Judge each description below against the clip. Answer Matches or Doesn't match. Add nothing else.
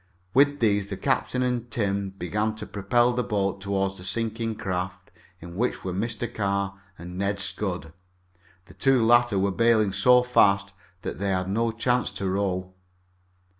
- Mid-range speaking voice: Doesn't match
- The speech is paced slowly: Doesn't match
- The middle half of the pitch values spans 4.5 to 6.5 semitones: Doesn't match